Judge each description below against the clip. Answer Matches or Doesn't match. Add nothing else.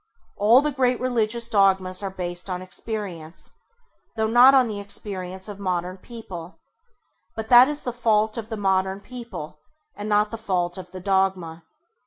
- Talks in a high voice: Matches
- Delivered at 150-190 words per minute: Matches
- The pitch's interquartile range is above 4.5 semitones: Doesn't match